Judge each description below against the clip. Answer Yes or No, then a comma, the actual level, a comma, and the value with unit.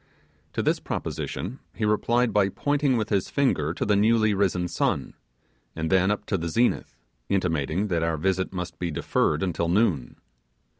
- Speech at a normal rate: Yes, average, 165 wpm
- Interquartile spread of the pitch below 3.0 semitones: No, average, 4.1 semitones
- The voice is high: No, very low, 95 Hz